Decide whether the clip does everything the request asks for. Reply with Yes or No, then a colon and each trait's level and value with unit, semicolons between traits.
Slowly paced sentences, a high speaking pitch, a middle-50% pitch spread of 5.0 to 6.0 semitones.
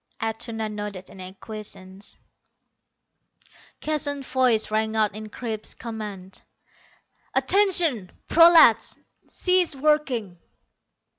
Yes: slow, 80 wpm; high, 220 Hz; wide, 5.5 semitones